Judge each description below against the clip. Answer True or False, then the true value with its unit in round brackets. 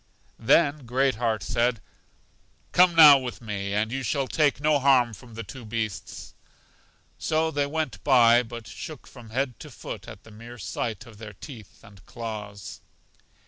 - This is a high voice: False (120 Hz)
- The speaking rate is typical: True (165 wpm)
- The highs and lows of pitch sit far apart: False (4.0 semitones)